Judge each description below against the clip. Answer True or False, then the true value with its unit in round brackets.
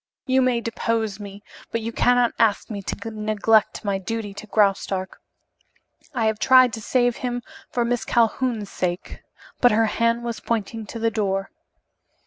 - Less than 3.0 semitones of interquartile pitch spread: True (2.4 semitones)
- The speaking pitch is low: False (225 Hz)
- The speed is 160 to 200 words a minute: True (165 wpm)